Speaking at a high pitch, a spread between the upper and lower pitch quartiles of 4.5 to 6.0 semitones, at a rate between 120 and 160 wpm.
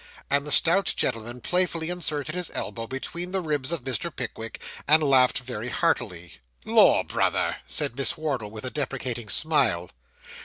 No: low, 135 Hz; average, 5.1 semitones; average, 155 wpm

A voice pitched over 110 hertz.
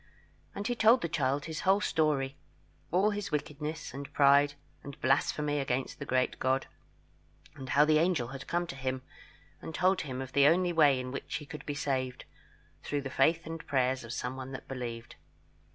Yes: medium, 140 Hz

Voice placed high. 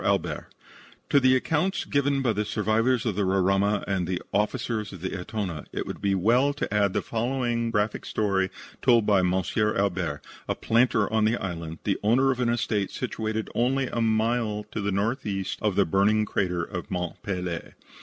No: low, 105 Hz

